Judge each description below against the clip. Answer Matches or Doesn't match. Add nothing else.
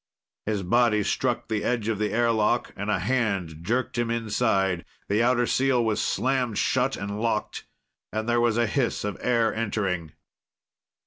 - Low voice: Matches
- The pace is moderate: Matches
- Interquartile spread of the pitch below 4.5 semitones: Matches